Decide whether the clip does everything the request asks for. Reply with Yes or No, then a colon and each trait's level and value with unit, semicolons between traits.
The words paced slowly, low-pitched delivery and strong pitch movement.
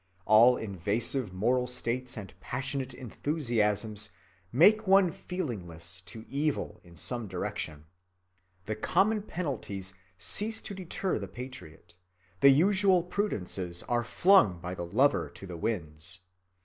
Yes: slow, 125 wpm; low, 120 Hz; wide, 8.5 semitones